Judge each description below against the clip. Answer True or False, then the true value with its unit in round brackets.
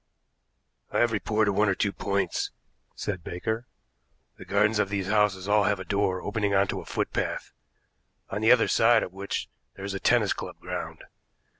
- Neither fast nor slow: True (175 wpm)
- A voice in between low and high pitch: False (100 Hz)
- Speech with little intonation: True (1.6 semitones)